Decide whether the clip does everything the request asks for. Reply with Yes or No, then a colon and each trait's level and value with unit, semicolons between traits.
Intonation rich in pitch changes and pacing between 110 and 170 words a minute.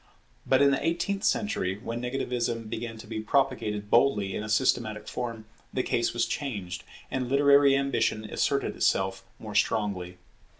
No: average, 4.2 semitones; average, 155 wpm